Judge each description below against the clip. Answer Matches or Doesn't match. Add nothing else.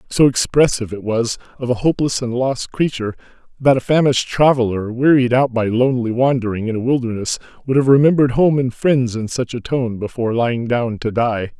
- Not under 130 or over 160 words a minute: Doesn't match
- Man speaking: Matches